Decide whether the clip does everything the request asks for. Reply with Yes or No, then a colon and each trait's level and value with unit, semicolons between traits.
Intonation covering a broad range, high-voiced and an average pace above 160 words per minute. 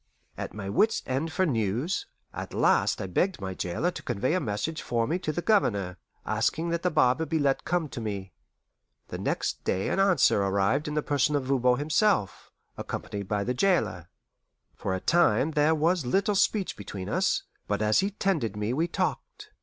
No: wide, 8.4 semitones; medium, 140 Hz; average, 190 wpm